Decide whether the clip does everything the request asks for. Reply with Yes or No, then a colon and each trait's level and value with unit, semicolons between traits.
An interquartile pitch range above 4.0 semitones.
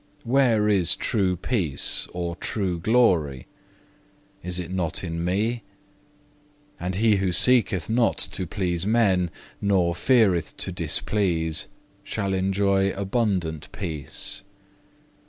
No: average, 3.6 semitones